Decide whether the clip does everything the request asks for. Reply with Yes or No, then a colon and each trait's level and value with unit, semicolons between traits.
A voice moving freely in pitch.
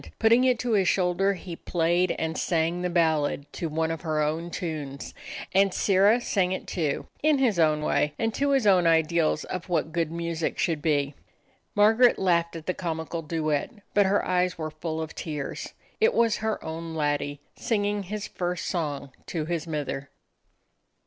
No: average, 3.7 semitones